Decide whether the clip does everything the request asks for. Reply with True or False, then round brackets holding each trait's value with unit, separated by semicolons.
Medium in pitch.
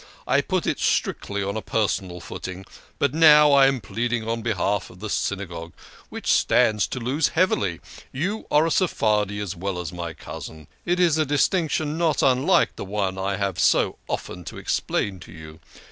False (105 Hz)